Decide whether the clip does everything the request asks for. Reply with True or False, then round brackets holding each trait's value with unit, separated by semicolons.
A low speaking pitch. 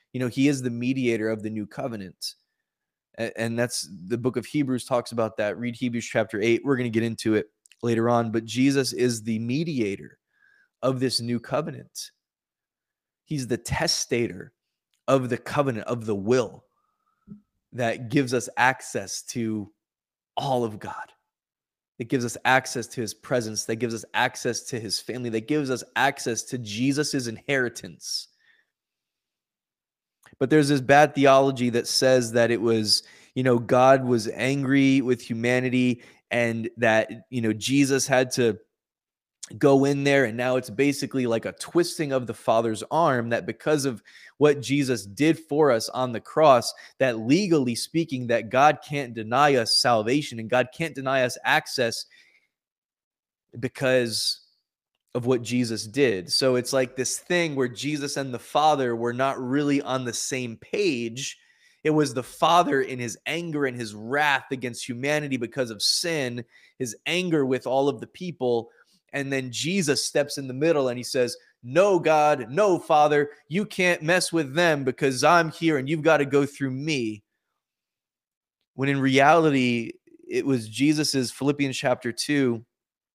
True (130 Hz)